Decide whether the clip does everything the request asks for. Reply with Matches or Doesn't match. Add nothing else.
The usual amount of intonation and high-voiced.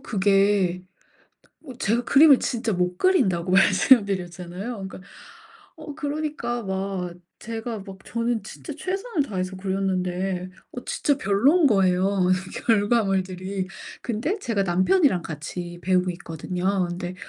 Matches